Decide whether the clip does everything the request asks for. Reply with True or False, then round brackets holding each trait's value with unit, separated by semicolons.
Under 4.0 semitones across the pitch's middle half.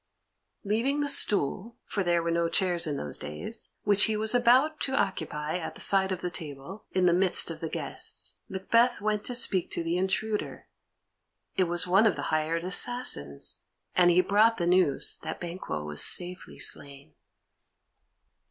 False (4.3 semitones)